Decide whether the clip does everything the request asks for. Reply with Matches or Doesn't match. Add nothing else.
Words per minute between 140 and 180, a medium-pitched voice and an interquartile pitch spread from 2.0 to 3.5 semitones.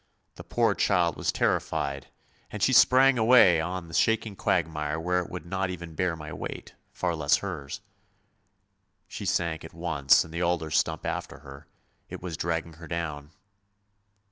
Doesn't match